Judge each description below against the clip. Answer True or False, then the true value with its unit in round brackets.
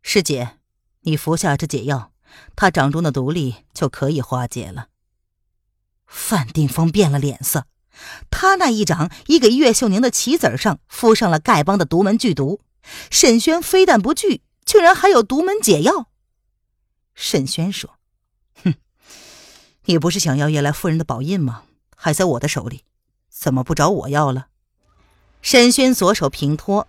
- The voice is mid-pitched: True (155 Hz)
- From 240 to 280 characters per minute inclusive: False (225 characters per minute)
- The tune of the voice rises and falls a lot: True (8.3 semitones)